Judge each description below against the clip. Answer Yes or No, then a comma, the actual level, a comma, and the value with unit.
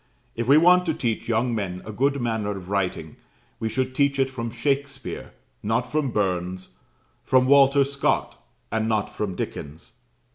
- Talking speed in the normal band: Yes, average, 160 wpm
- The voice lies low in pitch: Yes, low, 120 Hz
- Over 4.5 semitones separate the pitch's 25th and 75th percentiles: Yes, average, 5.0 semitones